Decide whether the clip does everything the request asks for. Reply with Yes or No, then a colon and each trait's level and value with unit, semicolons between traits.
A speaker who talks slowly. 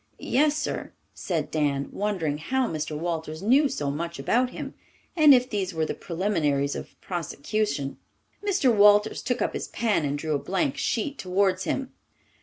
No: average, 165 wpm